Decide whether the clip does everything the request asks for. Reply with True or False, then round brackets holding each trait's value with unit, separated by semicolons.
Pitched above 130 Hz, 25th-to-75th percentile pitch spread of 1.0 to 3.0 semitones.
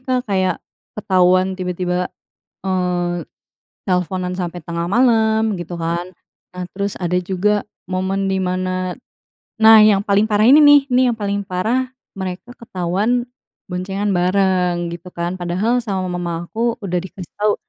True (185 Hz; 2.7 semitones)